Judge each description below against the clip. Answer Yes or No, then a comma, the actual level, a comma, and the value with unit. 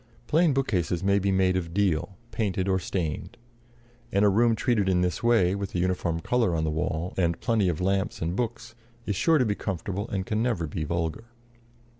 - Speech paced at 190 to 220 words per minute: Yes, average, 200 wpm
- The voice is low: Yes, very low, 95 Hz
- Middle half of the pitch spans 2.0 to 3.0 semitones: No, average, 3.9 semitones